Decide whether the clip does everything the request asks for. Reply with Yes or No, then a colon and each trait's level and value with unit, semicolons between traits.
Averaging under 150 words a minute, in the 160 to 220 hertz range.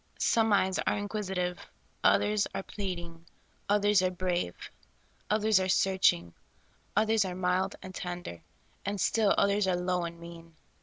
Yes: average, 140 wpm; medium, 185 Hz